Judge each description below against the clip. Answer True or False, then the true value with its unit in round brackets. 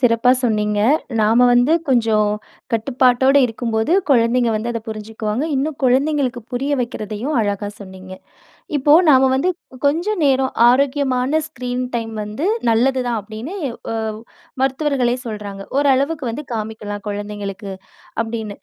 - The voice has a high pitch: True (245 Hz)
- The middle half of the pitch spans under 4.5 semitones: True (3.8 semitones)